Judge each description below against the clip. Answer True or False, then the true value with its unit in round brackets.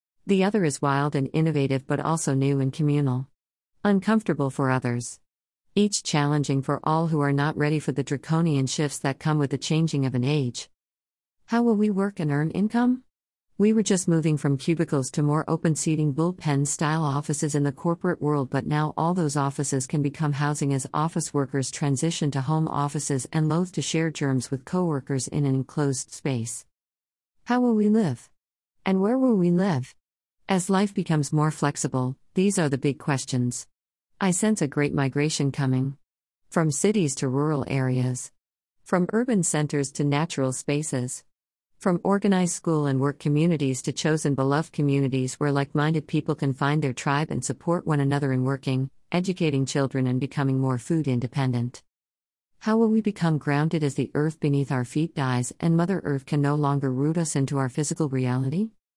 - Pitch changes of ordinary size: True (3.3 semitones)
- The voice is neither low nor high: True (145 Hz)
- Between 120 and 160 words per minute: False (180 wpm)